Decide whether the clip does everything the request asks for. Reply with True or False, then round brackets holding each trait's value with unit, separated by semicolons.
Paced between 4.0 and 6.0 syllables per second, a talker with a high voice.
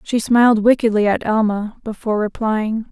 True (5.2 syllables/s; 220 Hz)